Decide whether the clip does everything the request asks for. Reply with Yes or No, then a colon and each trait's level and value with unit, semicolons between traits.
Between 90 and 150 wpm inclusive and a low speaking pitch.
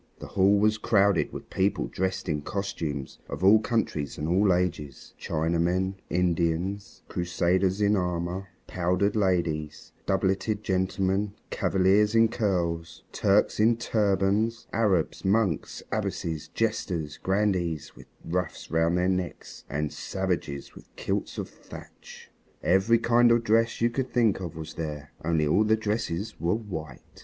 Yes: slow, 135 wpm; very low, 95 Hz